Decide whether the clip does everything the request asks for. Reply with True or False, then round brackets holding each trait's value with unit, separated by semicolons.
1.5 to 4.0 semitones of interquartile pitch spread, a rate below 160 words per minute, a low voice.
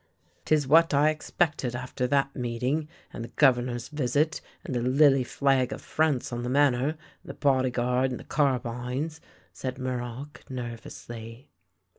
True (2.9 semitones; 150 wpm; 130 Hz)